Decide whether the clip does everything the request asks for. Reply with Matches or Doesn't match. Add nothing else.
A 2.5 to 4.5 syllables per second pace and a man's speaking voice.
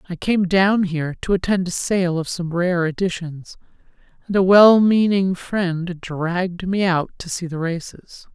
Doesn't match